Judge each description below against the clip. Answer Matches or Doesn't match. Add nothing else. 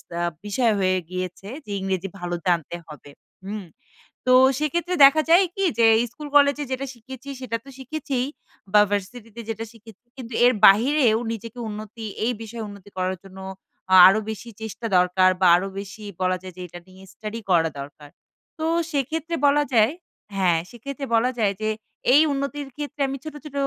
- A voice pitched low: Doesn't match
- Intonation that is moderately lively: Doesn't match